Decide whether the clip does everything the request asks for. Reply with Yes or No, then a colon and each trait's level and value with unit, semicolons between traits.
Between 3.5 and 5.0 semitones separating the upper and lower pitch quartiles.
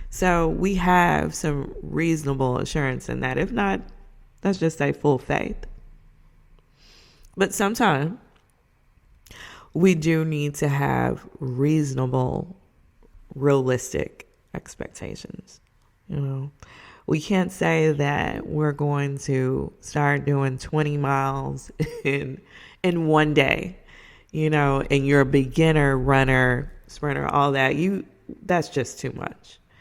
No: average, 2.7 semitones